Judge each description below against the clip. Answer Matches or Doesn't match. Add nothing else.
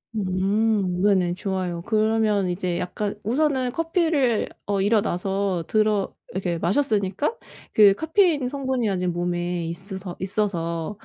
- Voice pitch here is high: Matches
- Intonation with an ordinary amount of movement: Matches